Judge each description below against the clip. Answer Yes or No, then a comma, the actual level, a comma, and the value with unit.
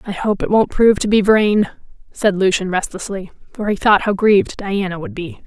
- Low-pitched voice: No, high, 200 Hz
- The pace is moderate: No, fast, 210 wpm